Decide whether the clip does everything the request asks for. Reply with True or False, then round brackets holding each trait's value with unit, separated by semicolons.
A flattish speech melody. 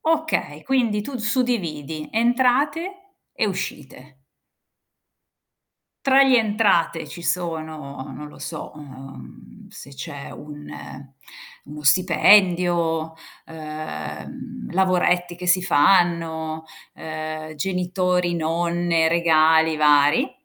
False (4.2 semitones)